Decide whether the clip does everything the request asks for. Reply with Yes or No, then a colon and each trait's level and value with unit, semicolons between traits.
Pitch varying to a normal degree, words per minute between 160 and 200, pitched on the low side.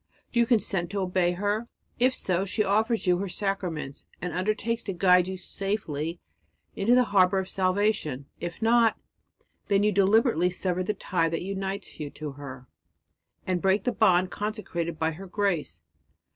No: average, 3.1 semitones; average, 165 wpm; high, 190 Hz